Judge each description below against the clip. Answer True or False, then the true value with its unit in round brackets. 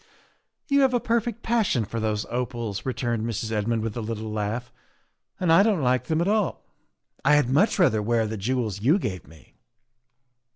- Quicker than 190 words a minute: True (200 wpm)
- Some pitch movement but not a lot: False (7.8 semitones)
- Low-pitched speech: True (120 Hz)